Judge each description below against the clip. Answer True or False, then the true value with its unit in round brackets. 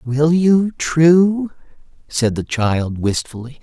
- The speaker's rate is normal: False (115 wpm)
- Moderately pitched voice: True (145 Hz)